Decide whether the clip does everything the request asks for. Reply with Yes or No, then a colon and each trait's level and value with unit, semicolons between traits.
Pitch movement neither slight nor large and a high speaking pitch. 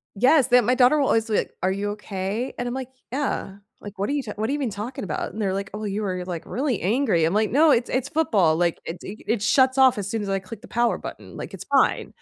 Yes: average, 4.5 semitones; high, 220 Hz